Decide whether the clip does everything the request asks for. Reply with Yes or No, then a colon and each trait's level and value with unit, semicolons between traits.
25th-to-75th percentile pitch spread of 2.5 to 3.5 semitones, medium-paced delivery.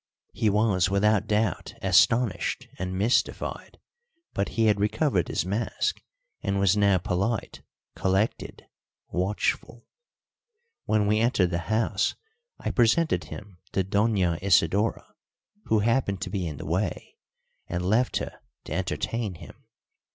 No: average, 3.0 semitones; slow, 130 wpm